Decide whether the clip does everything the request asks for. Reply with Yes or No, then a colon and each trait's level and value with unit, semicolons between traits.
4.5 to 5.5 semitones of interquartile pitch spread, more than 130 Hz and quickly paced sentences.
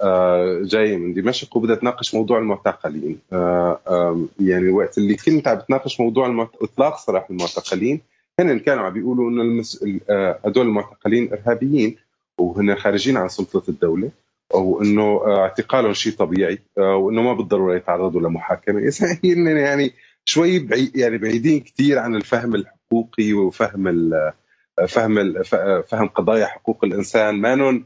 No: average, 4.8 semitones; low, 110 Hz; fast, 145 wpm